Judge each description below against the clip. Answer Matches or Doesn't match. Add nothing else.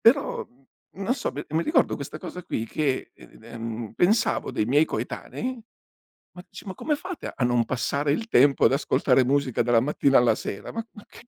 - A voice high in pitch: Doesn't match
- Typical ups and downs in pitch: Doesn't match